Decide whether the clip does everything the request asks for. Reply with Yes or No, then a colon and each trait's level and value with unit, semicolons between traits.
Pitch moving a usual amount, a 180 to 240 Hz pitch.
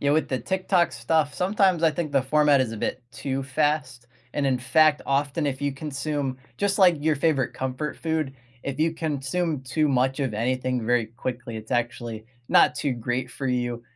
No: average, 3.7 semitones; low, 135 Hz